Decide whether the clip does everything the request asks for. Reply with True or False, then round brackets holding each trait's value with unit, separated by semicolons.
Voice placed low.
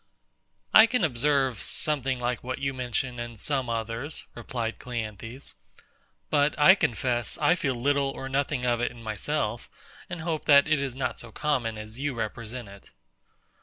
True (125 Hz)